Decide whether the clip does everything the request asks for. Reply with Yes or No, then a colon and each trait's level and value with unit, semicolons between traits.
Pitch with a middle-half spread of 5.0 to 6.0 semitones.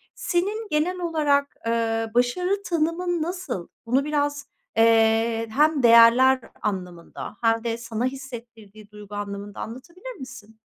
Yes: wide, 5.6 semitones